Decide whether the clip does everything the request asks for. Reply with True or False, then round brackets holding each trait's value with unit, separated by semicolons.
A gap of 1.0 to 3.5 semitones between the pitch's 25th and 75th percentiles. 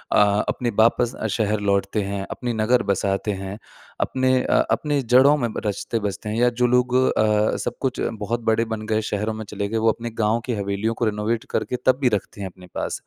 True (2.8 semitones)